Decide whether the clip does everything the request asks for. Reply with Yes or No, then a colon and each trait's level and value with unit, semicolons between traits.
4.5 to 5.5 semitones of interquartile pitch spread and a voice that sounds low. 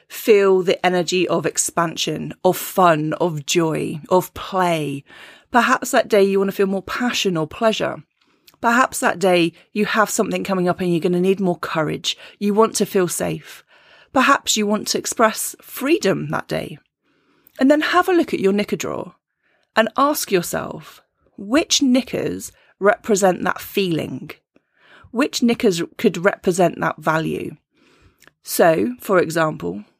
No: average, 5.1 semitones; high, 200 Hz